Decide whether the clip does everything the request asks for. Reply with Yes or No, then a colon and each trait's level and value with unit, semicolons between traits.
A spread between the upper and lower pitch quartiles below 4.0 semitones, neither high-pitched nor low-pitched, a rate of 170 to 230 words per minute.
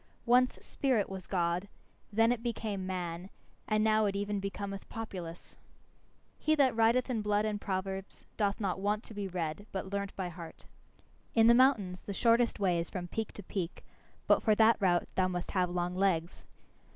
No: average, 3.2 semitones; high, 200 Hz; average, 180 wpm